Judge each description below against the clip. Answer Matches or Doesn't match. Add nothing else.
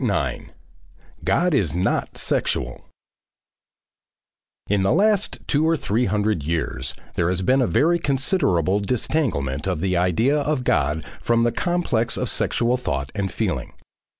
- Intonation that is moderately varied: Doesn't match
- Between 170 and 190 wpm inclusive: Doesn't match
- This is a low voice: Matches